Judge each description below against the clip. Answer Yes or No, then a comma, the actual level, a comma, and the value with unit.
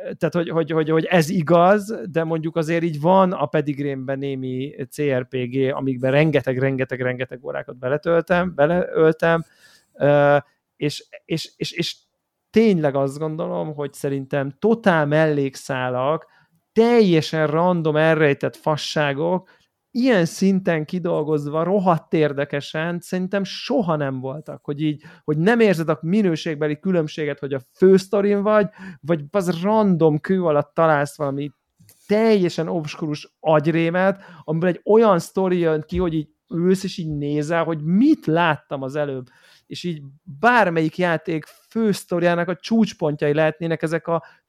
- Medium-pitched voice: Yes, medium, 160 Hz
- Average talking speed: Yes, average, 130 wpm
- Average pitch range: Yes, average, 3.7 semitones